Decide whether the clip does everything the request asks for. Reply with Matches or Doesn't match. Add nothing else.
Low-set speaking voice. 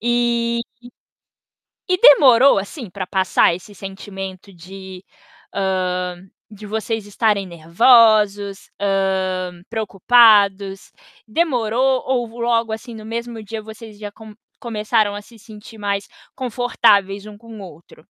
Doesn't match